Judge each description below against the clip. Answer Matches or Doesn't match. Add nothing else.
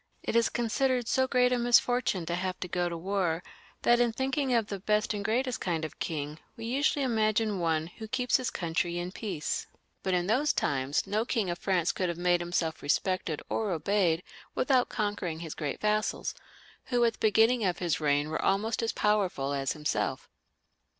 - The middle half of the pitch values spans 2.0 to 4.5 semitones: Doesn't match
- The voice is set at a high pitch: Matches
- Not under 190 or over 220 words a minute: Matches